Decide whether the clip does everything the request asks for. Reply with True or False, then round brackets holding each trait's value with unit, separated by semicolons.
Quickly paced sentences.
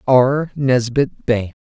False (110 wpm)